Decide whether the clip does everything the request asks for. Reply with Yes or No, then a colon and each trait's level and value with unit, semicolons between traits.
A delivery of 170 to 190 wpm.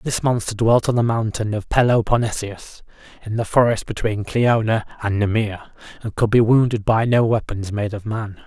Yes: average, 175 wpm